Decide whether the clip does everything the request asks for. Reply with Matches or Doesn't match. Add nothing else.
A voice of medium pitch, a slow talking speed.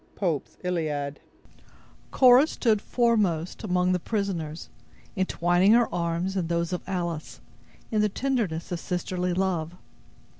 Matches